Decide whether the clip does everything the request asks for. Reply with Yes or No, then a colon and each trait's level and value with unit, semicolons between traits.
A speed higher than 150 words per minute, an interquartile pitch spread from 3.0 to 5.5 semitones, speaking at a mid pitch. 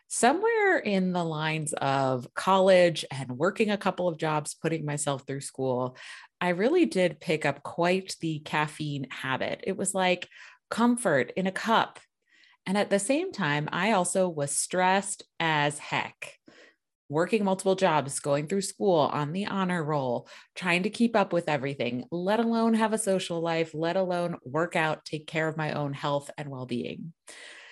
Yes: average, 170 wpm; average, 4.6 semitones; medium, 170 Hz